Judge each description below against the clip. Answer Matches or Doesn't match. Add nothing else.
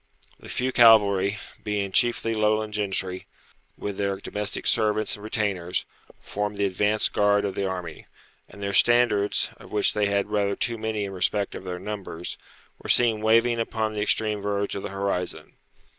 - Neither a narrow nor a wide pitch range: Doesn't match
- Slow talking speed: Doesn't match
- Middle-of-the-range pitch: Doesn't match